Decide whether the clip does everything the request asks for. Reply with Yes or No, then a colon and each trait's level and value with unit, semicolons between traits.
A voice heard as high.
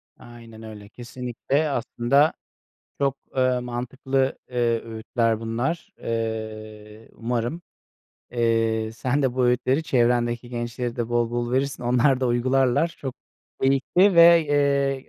No: low, 120 Hz